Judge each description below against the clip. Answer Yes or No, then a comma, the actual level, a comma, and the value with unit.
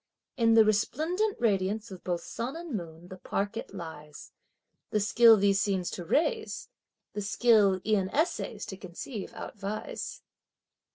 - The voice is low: No, high, 205 Hz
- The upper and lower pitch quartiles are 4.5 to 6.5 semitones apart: No, average, 3.7 semitones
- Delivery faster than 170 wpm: No, average, 145 wpm